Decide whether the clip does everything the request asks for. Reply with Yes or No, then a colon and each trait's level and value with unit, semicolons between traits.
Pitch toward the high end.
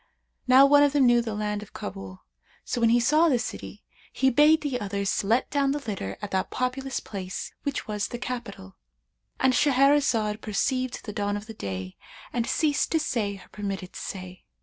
Yes: high, 230 Hz